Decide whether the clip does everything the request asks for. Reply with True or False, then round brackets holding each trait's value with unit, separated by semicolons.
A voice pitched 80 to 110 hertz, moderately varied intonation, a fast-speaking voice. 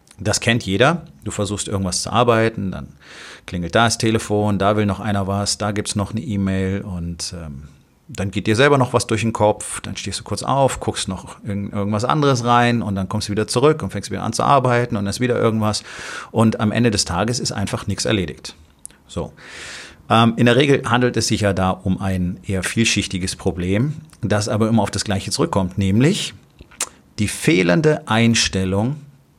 True (105 Hz; 3.4 semitones; 200 wpm)